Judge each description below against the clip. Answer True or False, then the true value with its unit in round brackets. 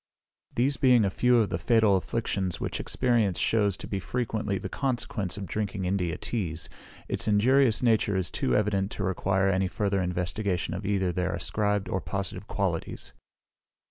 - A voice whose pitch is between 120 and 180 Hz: False (100 Hz)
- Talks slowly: False (165 wpm)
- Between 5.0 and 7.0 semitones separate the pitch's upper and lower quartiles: False (3.0 semitones)